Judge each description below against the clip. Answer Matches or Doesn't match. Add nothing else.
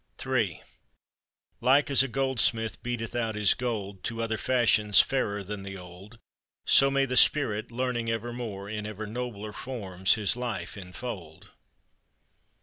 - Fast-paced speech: Doesn't match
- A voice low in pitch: Matches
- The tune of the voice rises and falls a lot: Doesn't match